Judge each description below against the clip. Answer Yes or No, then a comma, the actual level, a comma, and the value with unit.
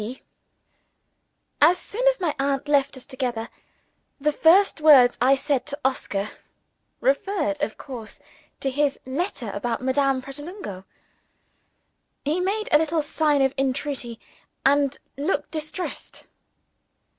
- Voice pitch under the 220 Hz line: No, very high, 280 Hz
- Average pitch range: Yes, average, 3.1 semitones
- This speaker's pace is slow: Yes, slow, 120 wpm